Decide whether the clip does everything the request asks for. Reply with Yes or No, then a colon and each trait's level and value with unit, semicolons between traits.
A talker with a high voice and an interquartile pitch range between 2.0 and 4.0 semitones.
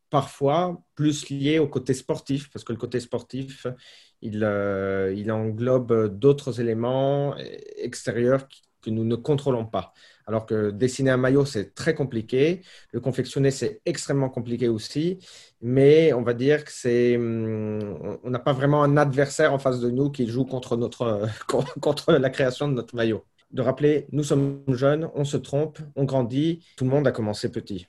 No: low, 130 Hz; average, 3.4 semitones